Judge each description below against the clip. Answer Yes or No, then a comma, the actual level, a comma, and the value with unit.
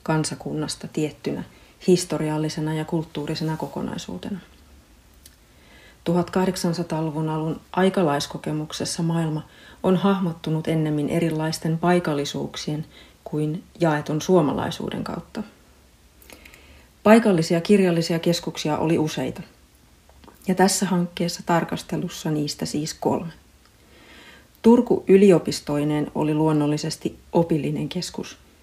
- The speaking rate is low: Yes, slow, 80 wpm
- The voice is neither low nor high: Yes, medium, 160 Hz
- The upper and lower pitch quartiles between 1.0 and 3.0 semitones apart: Yes, narrow, 2.6 semitones